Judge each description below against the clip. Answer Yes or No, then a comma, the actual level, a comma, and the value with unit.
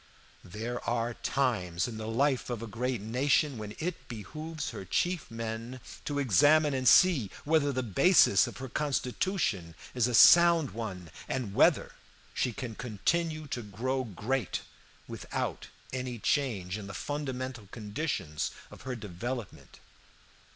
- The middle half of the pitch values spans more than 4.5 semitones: Yes, average, 4.9 semitones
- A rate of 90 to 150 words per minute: Yes, average, 140 wpm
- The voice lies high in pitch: No, low, 125 Hz